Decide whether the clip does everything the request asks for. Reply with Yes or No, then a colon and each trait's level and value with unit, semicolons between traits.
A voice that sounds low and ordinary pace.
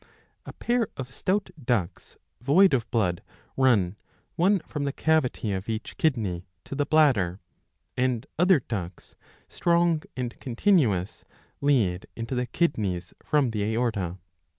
No: low, 125 Hz; slow, 130 wpm